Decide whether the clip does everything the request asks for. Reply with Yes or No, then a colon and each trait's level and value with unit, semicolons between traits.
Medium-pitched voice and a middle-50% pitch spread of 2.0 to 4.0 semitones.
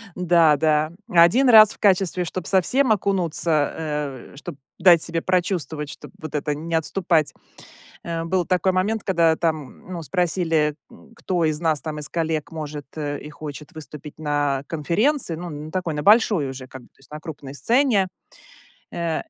Yes: medium, 165 Hz; average, 3.4 semitones